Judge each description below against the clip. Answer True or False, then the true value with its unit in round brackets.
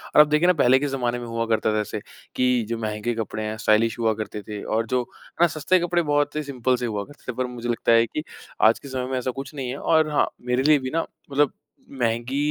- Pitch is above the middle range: False (125 Hz)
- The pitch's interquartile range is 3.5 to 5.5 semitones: True (4.1 semitones)